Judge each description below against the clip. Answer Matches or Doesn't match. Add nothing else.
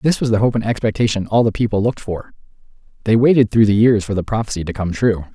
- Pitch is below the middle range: Matches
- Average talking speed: Doesn't match